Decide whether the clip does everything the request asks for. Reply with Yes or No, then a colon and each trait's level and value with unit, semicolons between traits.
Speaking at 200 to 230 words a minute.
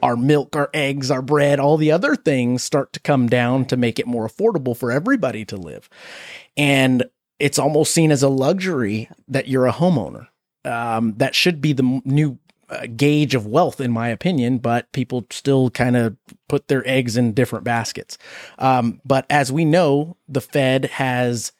No: average, 185 wpm